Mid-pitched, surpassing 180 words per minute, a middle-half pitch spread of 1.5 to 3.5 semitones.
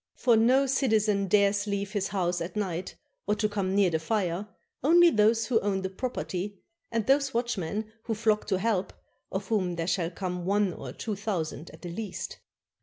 No: high, 205 Hz; average, 190 wpm; average, 3.1 semitones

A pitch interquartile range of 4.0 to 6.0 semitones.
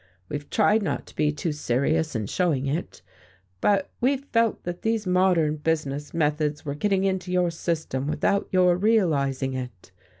Yes: average, 4.6 semitones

